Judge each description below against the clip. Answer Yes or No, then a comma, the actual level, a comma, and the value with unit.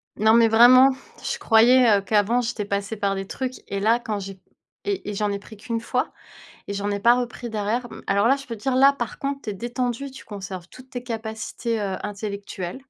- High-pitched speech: Yes, high, 225 Hz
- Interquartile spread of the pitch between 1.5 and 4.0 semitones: Yes, average, 3.5 semitones